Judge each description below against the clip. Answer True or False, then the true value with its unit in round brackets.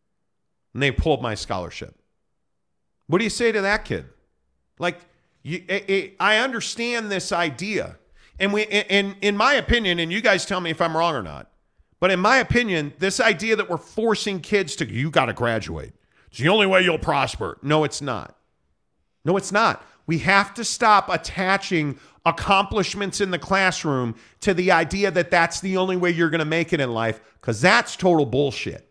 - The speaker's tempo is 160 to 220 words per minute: True (185 wpm)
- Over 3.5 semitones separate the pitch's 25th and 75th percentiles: True (4.3 semitones)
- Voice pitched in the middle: True (180 Hz)